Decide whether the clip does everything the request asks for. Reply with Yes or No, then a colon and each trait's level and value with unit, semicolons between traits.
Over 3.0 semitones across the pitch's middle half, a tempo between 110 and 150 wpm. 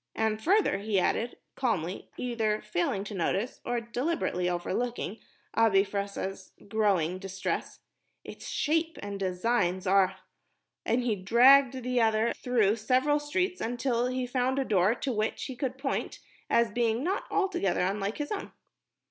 Yes: average, 4.4 semitones; average, 145 wpm